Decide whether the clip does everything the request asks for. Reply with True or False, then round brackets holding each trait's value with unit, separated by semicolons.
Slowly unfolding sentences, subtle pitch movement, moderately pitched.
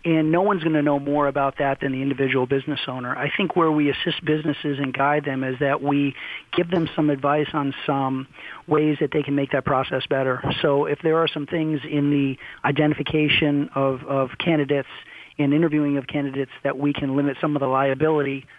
False (205 wpm; 1.6 semitones; 145 Hz)